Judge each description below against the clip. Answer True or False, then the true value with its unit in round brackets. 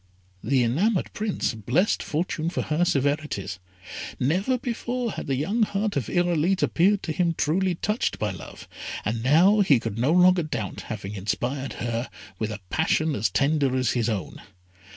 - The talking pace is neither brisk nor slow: True (165 wpm)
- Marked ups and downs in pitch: True (7.4 semitones)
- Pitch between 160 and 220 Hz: False (150 Hz)